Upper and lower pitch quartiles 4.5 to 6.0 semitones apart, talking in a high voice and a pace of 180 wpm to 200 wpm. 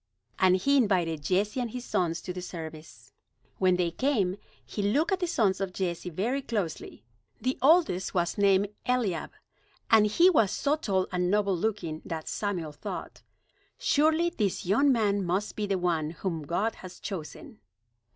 No: average, 4.8 semitones; high, 195 Hz; average, 165 wpm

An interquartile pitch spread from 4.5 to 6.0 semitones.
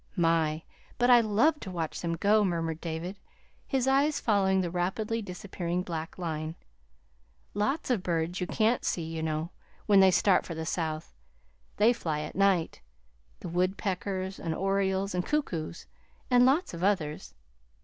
No: average, 4.0 semitones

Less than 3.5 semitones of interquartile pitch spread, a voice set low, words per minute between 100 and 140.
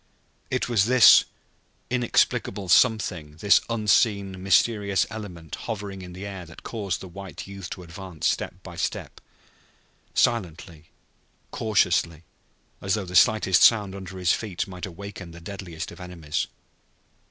Yes: average, 2.8 semitones; very low, 95 Hz; slow, 135 wpm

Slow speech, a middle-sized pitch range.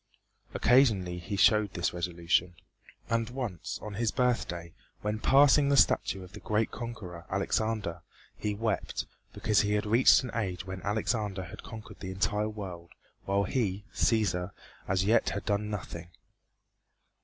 No: average, 145 wpm; average, 3.4 semitones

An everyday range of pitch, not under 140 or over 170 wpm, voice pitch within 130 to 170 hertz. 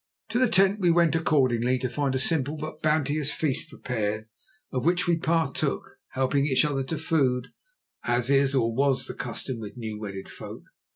No: average, 4.1 semitones; average, 180 wpm; low, 135 Hz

